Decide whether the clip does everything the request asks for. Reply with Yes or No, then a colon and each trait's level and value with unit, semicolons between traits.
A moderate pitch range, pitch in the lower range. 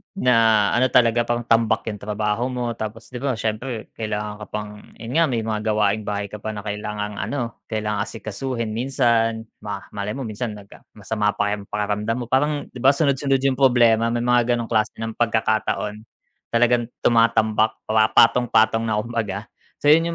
No: narrow, 2.3 semitones; low, 115 Hz